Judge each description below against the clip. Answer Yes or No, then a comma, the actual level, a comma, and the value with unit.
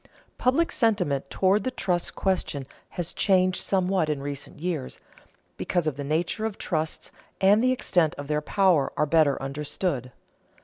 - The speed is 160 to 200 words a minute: No, average, 145 wpm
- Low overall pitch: No, medium, 175 Hz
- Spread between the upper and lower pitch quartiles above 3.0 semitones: Yes, average, 4.8 semitones